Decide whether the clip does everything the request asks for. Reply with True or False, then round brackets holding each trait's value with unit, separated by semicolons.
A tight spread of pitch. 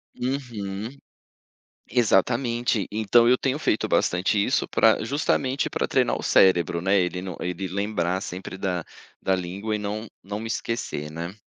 False (4.2 semitones)